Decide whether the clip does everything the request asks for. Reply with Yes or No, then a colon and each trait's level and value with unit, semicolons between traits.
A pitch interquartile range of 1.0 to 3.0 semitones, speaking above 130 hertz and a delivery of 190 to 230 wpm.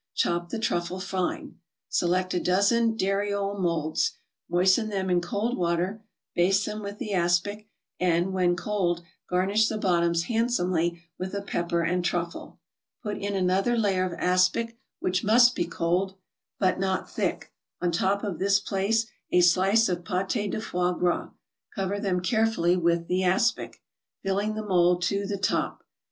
No: narrow, 2.5 semitones; medium, 185 Hz; average, 155 wpm